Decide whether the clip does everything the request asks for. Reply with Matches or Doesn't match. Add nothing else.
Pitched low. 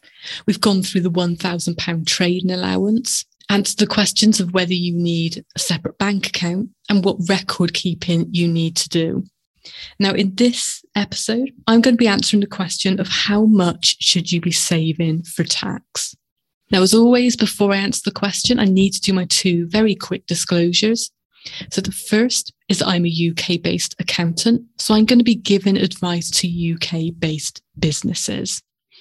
Doesn't match